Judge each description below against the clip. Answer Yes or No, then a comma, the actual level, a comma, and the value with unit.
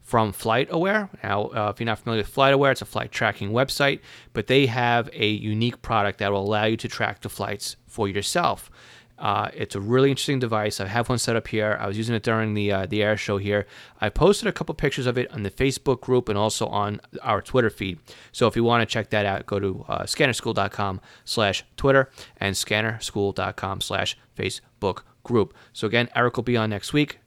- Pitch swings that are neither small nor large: Yes, average, 3.4 semitones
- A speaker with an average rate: No, fast, 215 wpm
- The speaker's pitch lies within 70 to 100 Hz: No, low, 110 Hz